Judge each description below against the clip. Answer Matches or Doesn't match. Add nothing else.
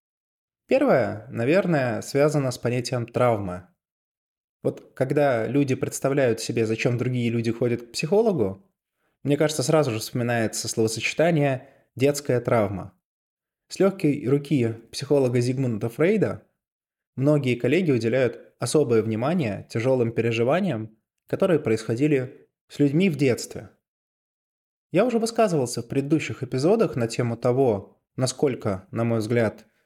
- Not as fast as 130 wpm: Matches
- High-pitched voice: Doesn't match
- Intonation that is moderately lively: Matches